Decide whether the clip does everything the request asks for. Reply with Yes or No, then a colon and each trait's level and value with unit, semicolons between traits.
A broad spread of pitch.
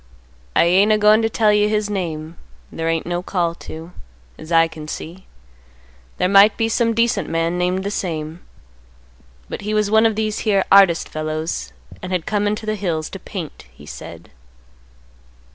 No: average, 4.3 semitones